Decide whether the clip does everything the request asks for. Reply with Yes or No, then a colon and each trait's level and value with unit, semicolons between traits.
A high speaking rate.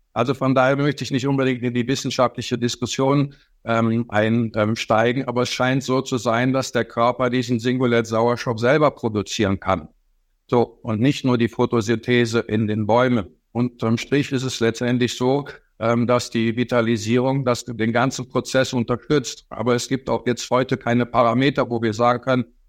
No: average, 170 wpm